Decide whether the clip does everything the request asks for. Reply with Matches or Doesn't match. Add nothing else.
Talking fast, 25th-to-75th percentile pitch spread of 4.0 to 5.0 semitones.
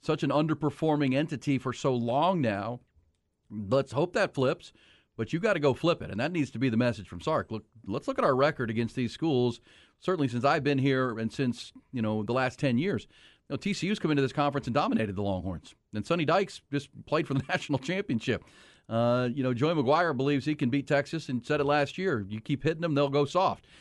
Matches